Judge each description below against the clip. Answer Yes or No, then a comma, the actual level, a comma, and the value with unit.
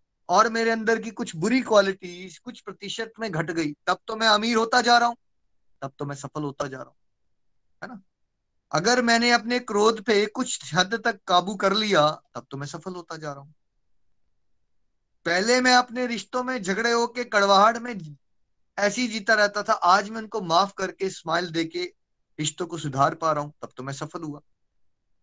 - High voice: Yes, high, 195 Hz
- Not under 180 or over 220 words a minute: Yes, fast, 190 wpm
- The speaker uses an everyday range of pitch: No, wide, 7.1 semitones